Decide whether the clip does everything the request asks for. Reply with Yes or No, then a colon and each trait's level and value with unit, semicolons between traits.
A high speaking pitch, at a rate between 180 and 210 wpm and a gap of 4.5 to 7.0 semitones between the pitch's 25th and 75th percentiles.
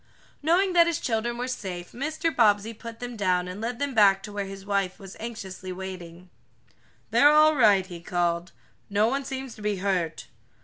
Yes: high, 205 Hz; average, 185 wpm; average, 4.9 semitones